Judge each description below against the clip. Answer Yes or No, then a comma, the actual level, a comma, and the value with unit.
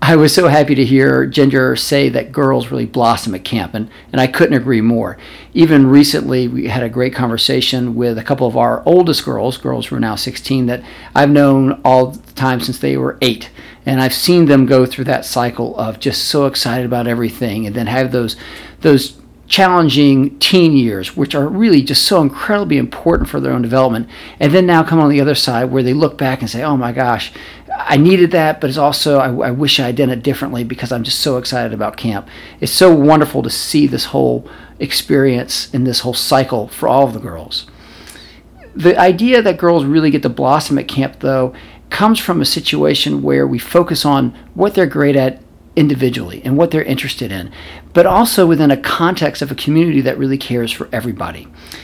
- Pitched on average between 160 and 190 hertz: No, low, 135 Hz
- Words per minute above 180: Yes, fast, 205 wpm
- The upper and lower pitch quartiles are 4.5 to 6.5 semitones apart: No, average, 3.5 semitones